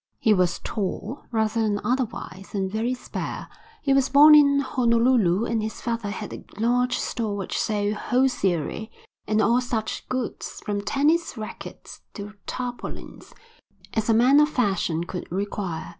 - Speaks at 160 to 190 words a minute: No, average, 150 wpm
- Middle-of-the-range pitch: No, high, 225 Hz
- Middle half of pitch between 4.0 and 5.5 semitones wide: No, average, 3.6 semitones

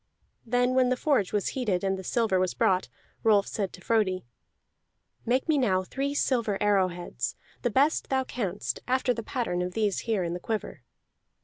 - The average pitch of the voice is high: Yes, high, 215 Hz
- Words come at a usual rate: Yes, average, 180 wpm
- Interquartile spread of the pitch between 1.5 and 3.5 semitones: No, average, 5.1 semitones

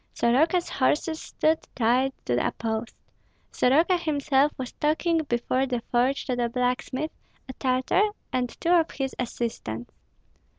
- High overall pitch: Yes, very high, 260 Hz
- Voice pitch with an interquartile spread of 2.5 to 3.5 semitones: No, average, 4.2 semitones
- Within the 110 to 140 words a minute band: Yes, slow, 135 wpm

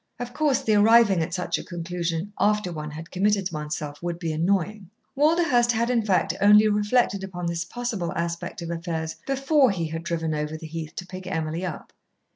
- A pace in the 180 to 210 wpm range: Yes, average, 190 wpm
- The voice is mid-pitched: Yes, medium, 180 Hz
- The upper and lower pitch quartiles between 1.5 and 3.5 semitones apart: No, average, 4.3 semitones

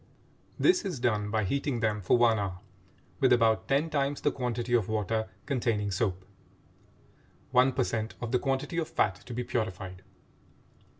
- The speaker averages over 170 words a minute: No, average, 165 wpm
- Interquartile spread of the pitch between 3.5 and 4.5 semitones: Yes, average, 4.0 semitones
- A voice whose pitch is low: Yes, low, 120 Hz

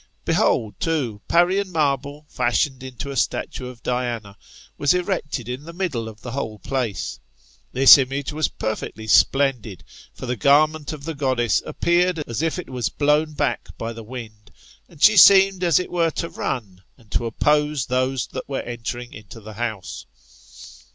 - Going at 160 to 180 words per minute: Yes, average, 165 wpm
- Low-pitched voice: Yes, low, 130 Hz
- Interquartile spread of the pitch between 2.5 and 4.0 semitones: No, average, 4.8 semitones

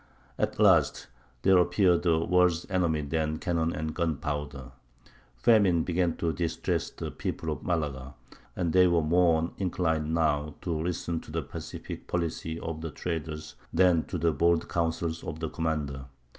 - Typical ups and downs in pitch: No, narrow, 1.9 semitones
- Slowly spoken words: No, average, 155 wpm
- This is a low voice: Yes, very low, 80 Hz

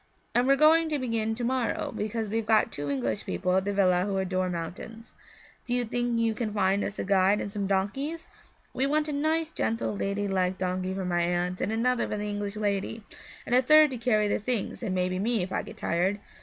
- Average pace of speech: No, fast, 225 wpm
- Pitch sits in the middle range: No, high, 210 Hz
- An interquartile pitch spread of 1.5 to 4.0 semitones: No, average, 4.4 semitones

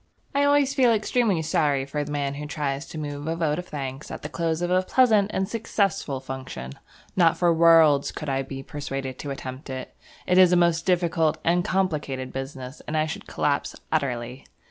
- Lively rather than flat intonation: No, average, 4.6 semitones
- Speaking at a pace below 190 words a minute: No, average, 195 wpm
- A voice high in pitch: No, medium, 155 Hz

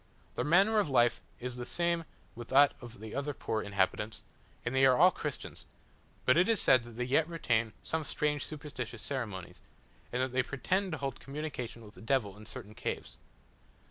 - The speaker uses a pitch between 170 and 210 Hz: No, low, 130 Hz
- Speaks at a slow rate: No, average, 190 wpm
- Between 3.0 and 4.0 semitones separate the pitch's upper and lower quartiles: No, average, 4.5 semitones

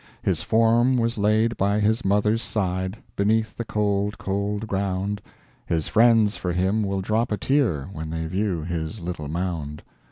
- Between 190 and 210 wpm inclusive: No, average, 160 wpm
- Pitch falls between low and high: No, low, 100 Hz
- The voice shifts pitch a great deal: No, average, 3.4 semitones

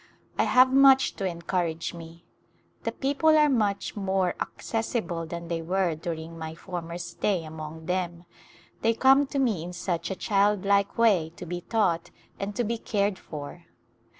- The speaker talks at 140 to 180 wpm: Yes, average, 165 wpm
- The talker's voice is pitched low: No, medium, 185 Hz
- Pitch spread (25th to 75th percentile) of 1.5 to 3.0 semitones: No, average, 4.7 semitones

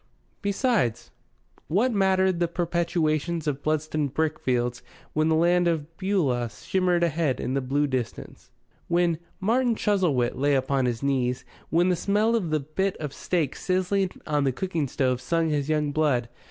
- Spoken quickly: No, average, 160 wpm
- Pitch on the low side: No, medium, 155 Hz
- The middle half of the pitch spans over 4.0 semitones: Yes, average, 4.7 semitones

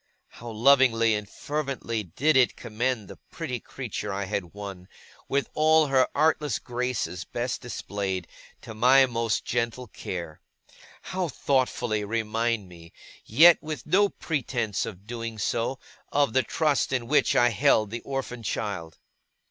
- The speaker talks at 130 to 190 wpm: Yes, average, 140 wpm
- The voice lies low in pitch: Yes, low, 120 Hz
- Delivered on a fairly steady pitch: No, average, 4.2 semitones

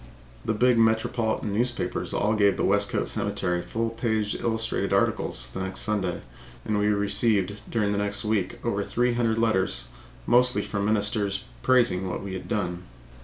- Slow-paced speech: No, average, 160 wpm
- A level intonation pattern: Yes, narrow, 2.3 semitones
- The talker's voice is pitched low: Yes, low, 105 Hz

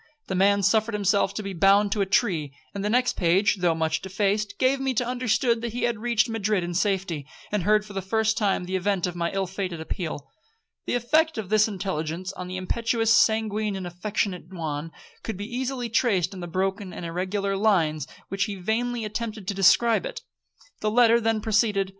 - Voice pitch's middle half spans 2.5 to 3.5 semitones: Yes, average, 3.2 semitones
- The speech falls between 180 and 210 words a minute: Yes, average, 200 wpm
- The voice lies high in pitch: Yes, high, 200 Hz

